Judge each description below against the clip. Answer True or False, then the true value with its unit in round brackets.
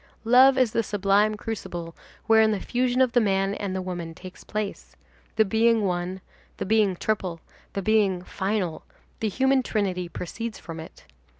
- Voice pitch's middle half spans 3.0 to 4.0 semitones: True (3.3 semitones)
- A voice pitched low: False (205 Hz)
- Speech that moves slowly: False (165 wpm)